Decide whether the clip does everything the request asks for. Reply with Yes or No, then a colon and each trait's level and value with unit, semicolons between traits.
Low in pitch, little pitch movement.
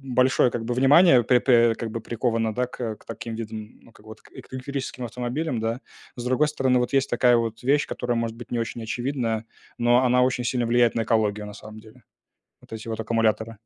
Yes: low, 120 Hz; narrow, 2.0 semitones